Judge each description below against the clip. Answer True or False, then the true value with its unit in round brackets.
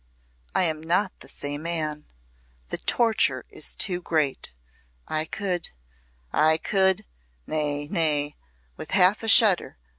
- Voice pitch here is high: False (165 Hz)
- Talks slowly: True (125 wpm)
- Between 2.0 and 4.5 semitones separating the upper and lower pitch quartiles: True (3.9 semitones)